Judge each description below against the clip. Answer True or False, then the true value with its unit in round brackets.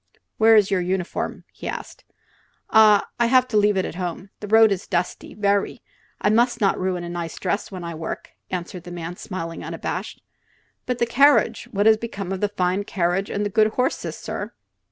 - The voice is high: True (200 Hz)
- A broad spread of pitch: False (3.5 semitones)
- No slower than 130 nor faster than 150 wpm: False (185 wpm)